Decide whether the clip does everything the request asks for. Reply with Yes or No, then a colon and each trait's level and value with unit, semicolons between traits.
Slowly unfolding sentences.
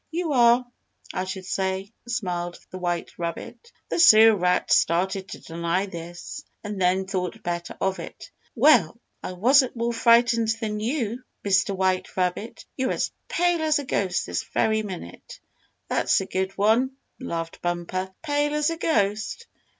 No: average, 155 wpm